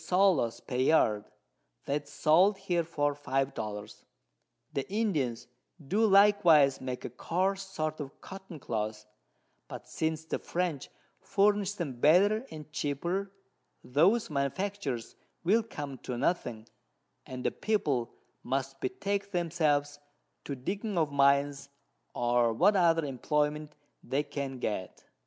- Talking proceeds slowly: Yes, slow, 125 wpm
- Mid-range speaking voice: Yes, medium, 150 Hz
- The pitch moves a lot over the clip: Yes, wide, 6.0 semitones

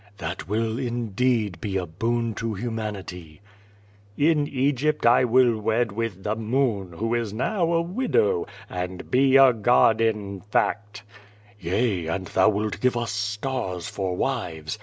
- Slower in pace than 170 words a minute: Yes, average, 150 wpm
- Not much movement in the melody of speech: No, average, 4.3 semitones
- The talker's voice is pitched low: Yes, low, 110 Hz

